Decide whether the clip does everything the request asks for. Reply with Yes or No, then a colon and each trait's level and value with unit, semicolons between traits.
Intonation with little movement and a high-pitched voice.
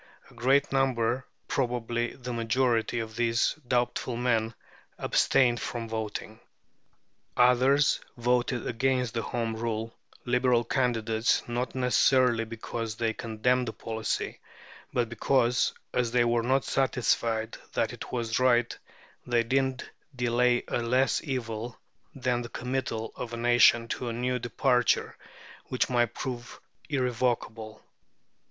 No: narrow, 1.7 semitones; low, 120 Hz